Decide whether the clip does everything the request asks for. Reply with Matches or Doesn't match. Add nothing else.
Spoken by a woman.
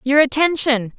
Matches